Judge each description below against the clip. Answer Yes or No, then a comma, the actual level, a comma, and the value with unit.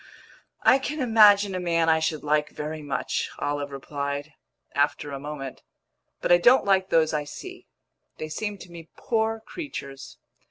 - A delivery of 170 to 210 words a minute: No, average, 160 wpm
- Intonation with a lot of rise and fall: Yes, wide, 5.8 semitones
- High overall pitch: No, medium, 160 Hz